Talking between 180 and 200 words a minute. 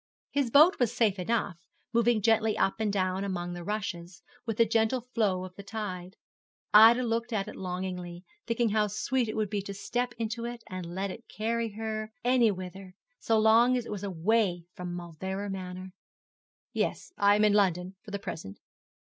Yes: average, 185 wpm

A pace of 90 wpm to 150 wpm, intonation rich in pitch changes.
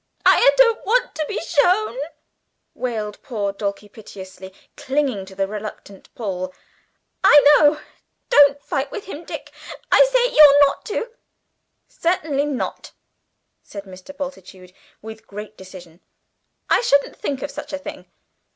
Yes: slow, 135 wpm; wide, 6.9 semitones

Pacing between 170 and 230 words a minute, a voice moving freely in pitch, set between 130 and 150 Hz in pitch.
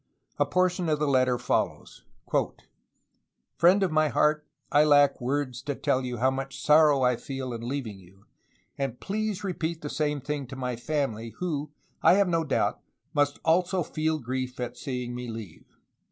No: average, 175 wpm; average, 3.8 semitones; medium, 140 Hz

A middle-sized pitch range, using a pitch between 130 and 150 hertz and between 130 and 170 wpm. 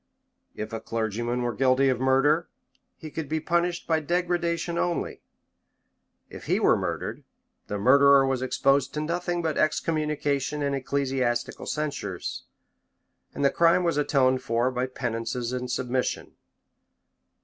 Yes: average, 4.0 semitones; low, 135 Hz; slow, 135 wpm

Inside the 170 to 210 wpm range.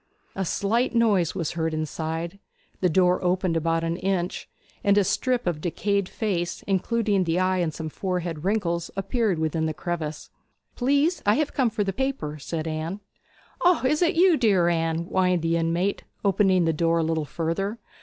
Yes: average, 175 wpm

